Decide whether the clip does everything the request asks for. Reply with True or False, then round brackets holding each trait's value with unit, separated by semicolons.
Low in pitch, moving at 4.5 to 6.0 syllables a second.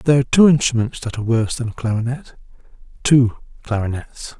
False (125 Hz; 6.3 syllables/s)